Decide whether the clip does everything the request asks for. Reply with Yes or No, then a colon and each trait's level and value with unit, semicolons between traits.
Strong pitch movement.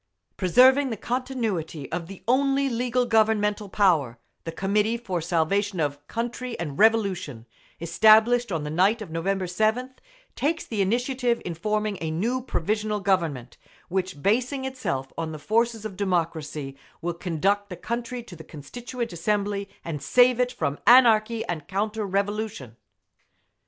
Yes: wide, 5.8 semitones